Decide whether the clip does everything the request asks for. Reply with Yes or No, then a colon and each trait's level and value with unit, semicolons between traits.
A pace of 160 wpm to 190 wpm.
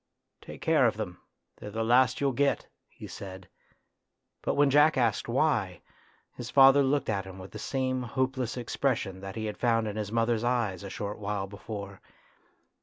Yes: average, 180 wpm